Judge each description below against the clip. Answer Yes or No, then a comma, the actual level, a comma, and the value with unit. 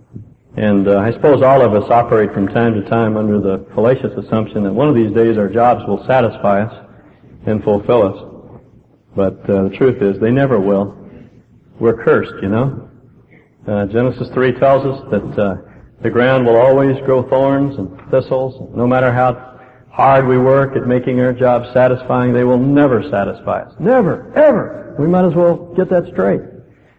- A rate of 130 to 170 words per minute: No, average, 180 wpm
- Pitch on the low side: Yes, low, 125 Hz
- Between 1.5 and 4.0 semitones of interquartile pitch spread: Yes, average, 3.7 semitones